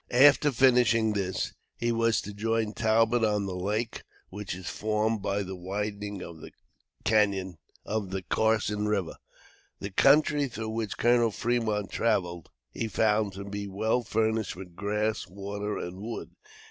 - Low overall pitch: Yes, low, 105 Hz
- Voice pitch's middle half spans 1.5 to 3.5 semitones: Yes, narrow, 2.4 semitones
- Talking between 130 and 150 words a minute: Yes, average, 140 wpm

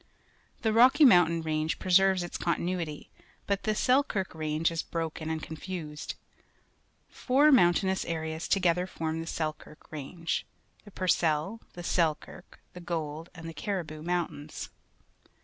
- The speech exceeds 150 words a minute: No, average, 140 wpm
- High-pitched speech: No, medium, 170 Hz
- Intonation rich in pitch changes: No, average, 3.1 semitones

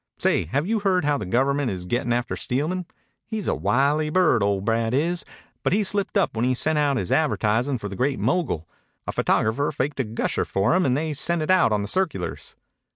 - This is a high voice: No, medium, 140 Hz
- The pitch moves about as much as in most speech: No, wide, 6.9 semitones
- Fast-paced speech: Yes, fast, 220 wpm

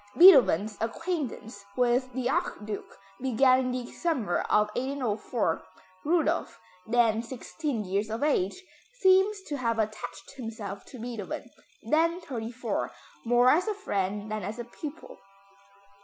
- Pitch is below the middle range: No, high, 245 Hz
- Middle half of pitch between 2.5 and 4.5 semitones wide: No, average, 5.3 semitones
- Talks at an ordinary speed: No, slow, 130 wpm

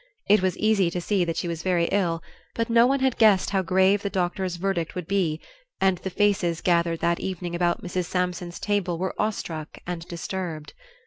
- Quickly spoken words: No, average, 195 wpm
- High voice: No, medium, 180 Hz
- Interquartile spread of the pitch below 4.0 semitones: Yes, narrow, 2.4 semitones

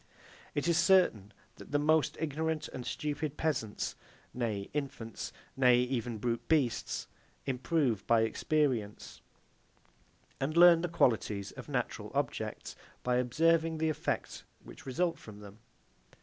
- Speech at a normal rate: No, slow, 125 wpm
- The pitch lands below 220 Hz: Yes, low, 135 Hz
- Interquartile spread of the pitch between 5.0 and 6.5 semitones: Yes, wide, 5.6 semitones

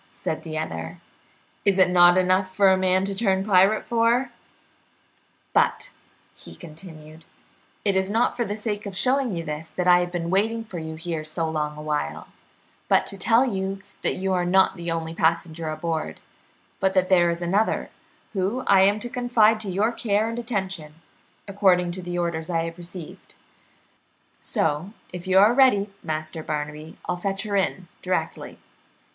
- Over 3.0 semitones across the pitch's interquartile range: Yes, average, 3.4 semitones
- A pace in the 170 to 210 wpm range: Yes, average, 175 wpm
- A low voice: No, medium, 185 Hz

